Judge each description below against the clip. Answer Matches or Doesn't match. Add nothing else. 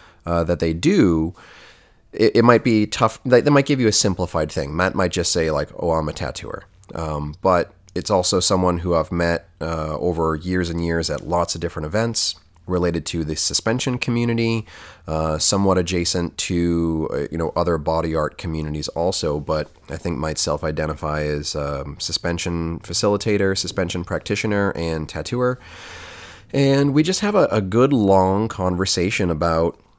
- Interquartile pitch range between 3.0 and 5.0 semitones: Matches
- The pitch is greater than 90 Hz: Doesn't match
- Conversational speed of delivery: Matches